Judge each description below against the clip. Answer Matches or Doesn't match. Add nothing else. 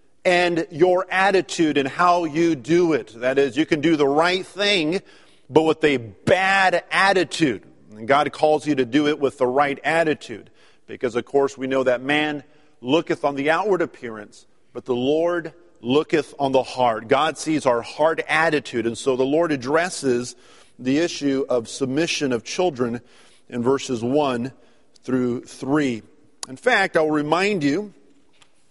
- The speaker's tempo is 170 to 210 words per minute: Doesn't match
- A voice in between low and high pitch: Matches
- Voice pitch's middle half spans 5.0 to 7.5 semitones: Doesn't match